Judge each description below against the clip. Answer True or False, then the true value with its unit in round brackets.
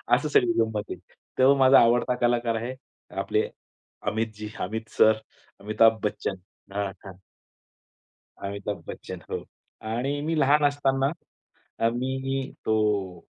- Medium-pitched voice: False (115 Hz)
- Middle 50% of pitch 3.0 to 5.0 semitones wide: True (3.9 semitones)